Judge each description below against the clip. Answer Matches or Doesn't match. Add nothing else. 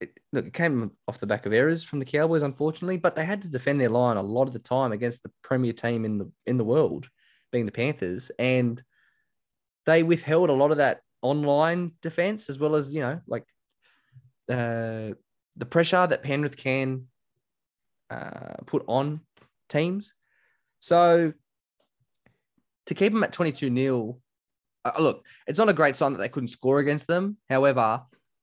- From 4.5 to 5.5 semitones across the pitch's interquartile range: Matches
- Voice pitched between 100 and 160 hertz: Matches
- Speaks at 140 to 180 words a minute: Matches